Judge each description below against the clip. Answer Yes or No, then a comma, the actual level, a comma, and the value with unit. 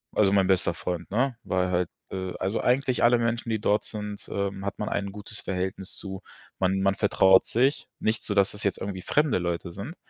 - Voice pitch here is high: No, low, 100 Hz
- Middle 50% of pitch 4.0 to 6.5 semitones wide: No, narrow, 2.6 semitones